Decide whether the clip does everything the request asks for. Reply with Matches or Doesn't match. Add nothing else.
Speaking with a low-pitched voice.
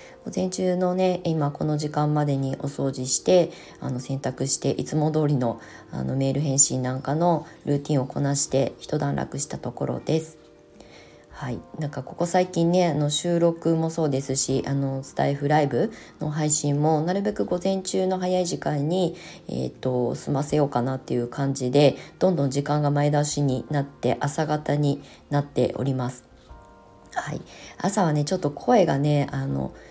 Doesn't match